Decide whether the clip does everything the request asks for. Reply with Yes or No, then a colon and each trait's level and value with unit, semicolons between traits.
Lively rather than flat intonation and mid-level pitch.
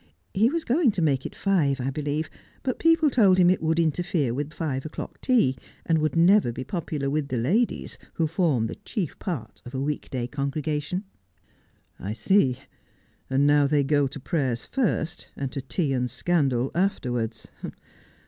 No: average, 5.0 semitones; medium, 150 Hz